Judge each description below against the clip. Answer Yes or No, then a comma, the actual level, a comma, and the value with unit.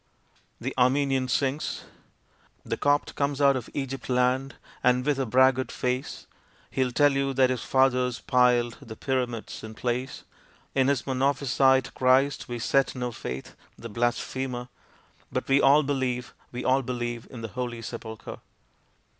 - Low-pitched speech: Yes, low, 130 Hz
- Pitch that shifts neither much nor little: No, narrow, 1.8 semitones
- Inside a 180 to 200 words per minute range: No, average, 145 wpm